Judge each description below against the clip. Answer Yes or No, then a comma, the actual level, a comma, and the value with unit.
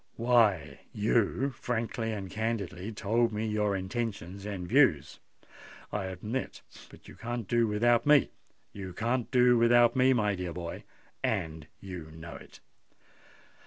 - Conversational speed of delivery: No, slow, 120 wpm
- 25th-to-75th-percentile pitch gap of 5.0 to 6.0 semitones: No, average, 4.1 semitones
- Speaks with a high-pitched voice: No, low, 110 Hz